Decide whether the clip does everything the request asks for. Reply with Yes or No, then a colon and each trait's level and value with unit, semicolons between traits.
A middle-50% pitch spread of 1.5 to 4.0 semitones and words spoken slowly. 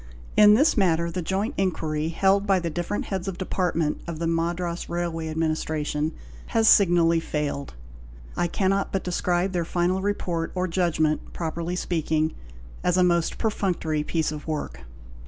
No: average, 2.7 semitones; average, 155 wpm